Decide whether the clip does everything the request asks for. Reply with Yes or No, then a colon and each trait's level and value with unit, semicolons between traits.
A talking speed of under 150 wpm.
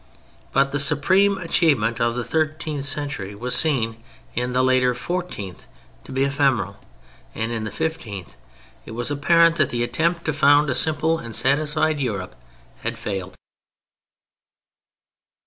Yes: average, 140 wpm